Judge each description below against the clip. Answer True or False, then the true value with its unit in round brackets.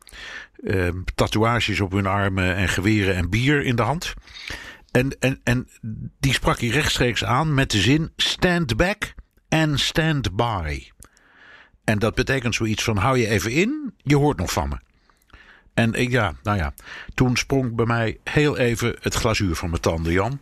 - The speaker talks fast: False (175 wpm)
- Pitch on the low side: True (115 Hz)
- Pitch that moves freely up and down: False (5.0 semitones)